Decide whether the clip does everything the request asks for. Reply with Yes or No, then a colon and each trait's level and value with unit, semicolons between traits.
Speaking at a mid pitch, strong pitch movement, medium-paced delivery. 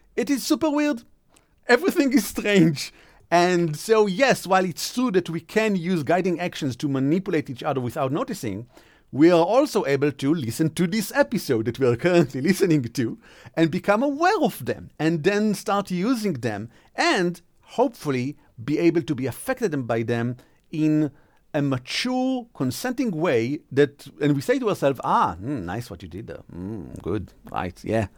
Yes: medium, 170 Hz; wide, 7.1 semitones; average, 175 wpm